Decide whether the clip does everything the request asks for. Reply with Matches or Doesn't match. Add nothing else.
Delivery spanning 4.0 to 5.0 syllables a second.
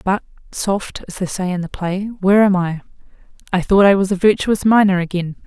Doesn't match